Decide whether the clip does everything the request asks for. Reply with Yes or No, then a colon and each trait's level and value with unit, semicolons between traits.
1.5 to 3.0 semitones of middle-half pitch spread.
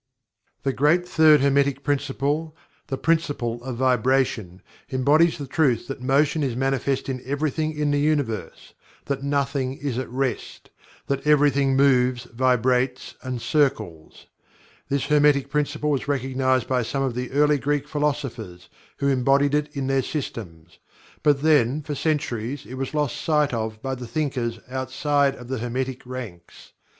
Yes: narrow, 2.4 semitones